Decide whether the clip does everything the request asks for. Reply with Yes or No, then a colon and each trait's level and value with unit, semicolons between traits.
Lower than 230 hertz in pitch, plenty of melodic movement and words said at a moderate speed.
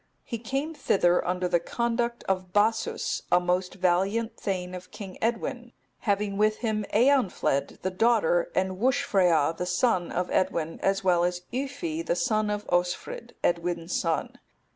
No: high, 190 Hz; average, 4.4 semitones; average, 150 wpm